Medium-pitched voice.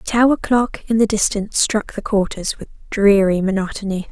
No: high, 210 Hz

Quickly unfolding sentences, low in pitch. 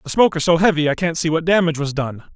No: fast, 305 wpm; medium, 165 Hz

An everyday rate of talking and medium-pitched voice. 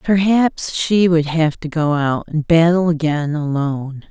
Yes: average, 160 wpm; medium, 160 Hz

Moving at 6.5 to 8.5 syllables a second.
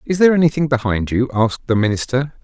Yes: 6.8 syllables/s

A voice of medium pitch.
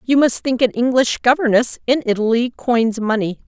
No: high, 240 Hz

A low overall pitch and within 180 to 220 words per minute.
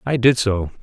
Yes: low, 115 Hz; fast, 215 wpm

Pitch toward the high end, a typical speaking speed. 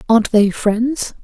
Yes: high, 225 Hz; average, 145 wpm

